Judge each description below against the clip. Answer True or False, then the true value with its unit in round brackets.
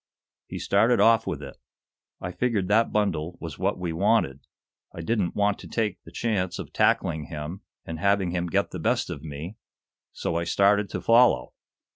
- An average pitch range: True (4.1 semitones)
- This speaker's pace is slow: False (180 wpm)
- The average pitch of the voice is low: True (95 Hz)